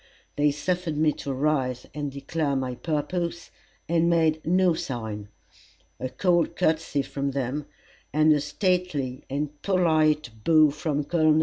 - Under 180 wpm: Yes, slow, 135 wpm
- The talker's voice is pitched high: No, medium, 150 Hz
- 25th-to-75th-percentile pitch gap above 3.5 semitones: No, average, 2.8 semitones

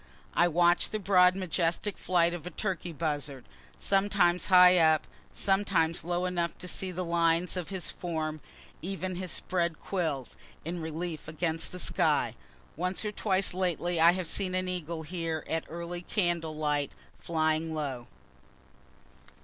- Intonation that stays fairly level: Yes, narrow, 2.2 semitones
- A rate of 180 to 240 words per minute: No, average, 150 wpm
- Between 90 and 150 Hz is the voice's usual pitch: No, medium, 175 Hz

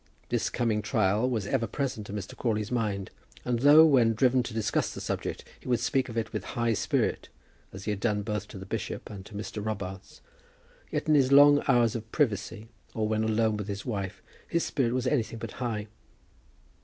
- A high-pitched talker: No, low, 110 Hz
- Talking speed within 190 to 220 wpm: Yes, fast, 205 wpm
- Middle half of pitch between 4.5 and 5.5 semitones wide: No, average, 3.2 semitones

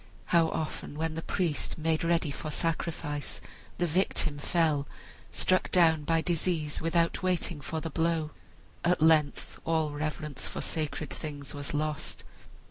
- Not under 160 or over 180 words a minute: No, average, 140 wpm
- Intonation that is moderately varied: No, narrow, 1.9 semitones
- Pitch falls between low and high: Yes, medium, 160 Hz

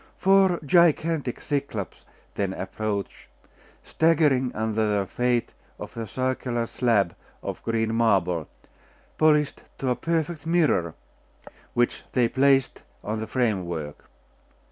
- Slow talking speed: Yes, slow, 110 wpm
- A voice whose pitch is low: Yes, low, 120 Hz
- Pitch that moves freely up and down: Yes, wide, 5.9 semitones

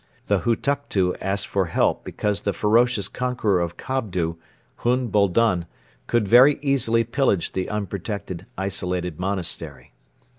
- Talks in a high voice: No, low, 100 Hz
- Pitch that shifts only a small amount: No, average, 4.6 semitones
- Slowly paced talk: Yes, slow, 120 wpm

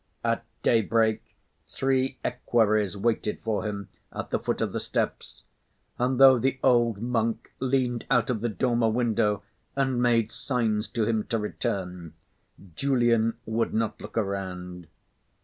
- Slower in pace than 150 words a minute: Yes, average, 140 wpm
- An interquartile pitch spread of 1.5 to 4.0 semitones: Yes, narrow, 2.6 semitones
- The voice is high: No, low, 115 Hz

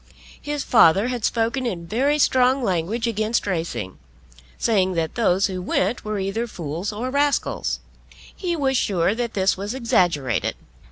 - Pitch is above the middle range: Yes, high, 215 Hz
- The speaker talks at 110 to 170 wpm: Yes, average, 150 wpm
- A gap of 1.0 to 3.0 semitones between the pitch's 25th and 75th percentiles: No, average, 5.2 semitones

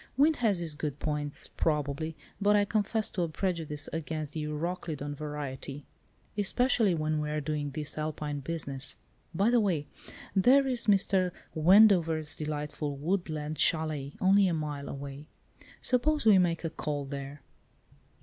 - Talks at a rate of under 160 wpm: Yes, average, 140 wpm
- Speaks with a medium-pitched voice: Yes, medium, 155 Hz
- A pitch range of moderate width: Yes, average, 4.5 semitones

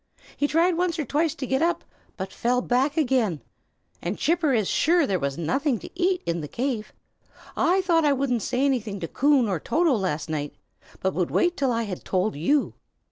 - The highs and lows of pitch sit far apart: Yes, wide, 8.3 semitones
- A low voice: No, very high, 260 Hz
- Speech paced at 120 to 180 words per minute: No, average, 200 wpm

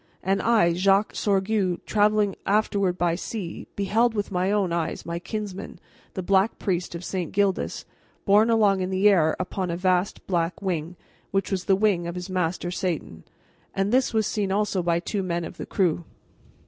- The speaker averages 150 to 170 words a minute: No, average, 180 wpm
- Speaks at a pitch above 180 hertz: Yes, high, 190 Hz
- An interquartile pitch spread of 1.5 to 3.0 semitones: Yes, narrow, 2.6 semitones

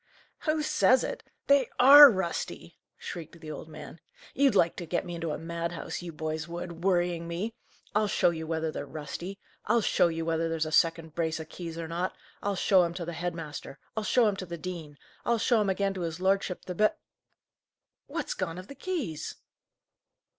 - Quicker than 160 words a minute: Yes, average, 200 wpm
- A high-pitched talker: No, medium, 170 Hz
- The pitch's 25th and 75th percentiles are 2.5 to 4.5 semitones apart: Yes, average, 3.4 semitones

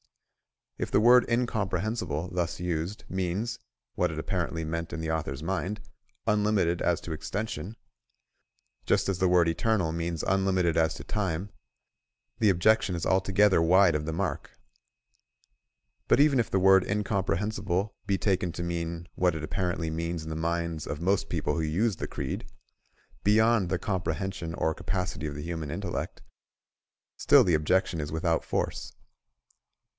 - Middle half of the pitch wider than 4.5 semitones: No, average, 3.1 semitones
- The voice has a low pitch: Yes, very low, 90 Hz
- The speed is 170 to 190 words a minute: No, average, 150 wpm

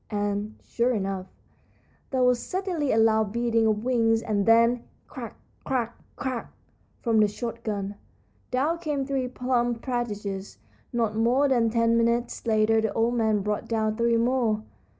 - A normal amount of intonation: No, narrow, 2.3 semitones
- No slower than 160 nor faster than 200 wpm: No, average, 150 wpm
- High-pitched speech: Yes, high, 230 Hz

